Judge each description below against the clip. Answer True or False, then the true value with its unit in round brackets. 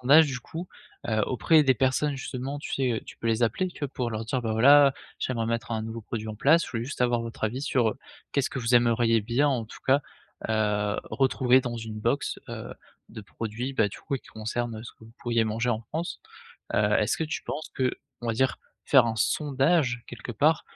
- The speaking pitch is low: True (120 Hz)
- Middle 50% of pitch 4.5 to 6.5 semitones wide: False (3.3 semitones)